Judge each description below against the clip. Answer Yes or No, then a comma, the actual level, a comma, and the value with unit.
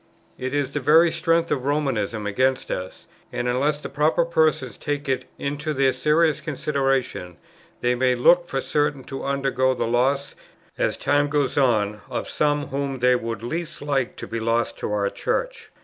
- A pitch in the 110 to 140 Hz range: Yes, low, 135 Hz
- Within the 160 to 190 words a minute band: Yes, average, 175 wpm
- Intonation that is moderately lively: Yes, average, 3.1 semitones